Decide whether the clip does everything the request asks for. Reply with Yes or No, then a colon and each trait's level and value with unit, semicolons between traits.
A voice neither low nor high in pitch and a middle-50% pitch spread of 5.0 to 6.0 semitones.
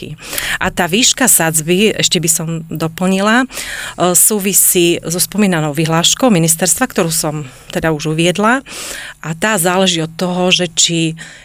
No: medium, 175 Hz; average, 2.9 semitones